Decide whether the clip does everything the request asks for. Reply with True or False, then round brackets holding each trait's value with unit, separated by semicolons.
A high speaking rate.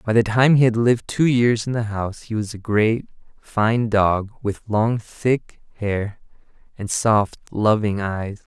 False (175 wpm)